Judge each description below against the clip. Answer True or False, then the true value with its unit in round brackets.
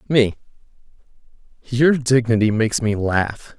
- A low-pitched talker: True (115 Hz)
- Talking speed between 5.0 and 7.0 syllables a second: False (4.2 syllables/s)